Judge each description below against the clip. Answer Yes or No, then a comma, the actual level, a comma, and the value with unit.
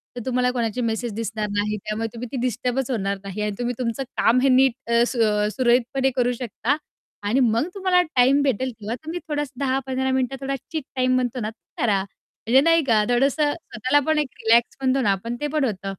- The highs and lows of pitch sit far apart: No, average, 3.1 semitones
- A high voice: Yes, very high, 250 Hz